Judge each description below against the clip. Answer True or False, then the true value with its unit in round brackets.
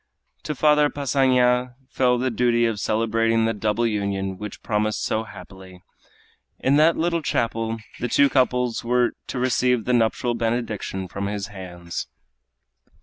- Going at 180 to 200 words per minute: False (145 wpm)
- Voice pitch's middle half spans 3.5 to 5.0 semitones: False (3.1 semitones)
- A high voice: False (115 Hz)